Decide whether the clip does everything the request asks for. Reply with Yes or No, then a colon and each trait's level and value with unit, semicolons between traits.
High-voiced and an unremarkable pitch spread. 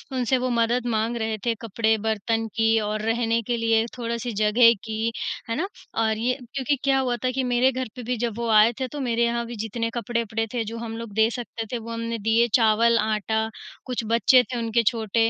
No: high, 230 Hz; narrow, 1.5 semitones